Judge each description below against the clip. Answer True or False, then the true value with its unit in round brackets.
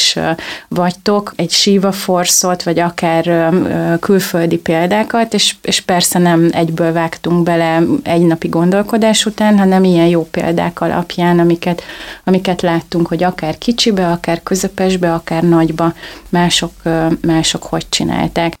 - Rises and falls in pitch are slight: True (2.0 semitones)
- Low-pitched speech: False (175 Hz)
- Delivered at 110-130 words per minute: True (125 wpm)